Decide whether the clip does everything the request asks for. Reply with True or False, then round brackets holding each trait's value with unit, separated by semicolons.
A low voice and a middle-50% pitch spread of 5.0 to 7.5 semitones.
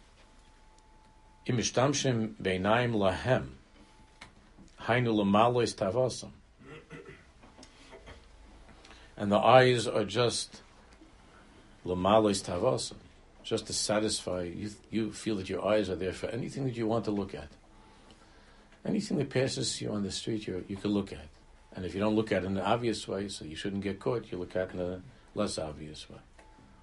False (105 Hz; 3.1 semitones)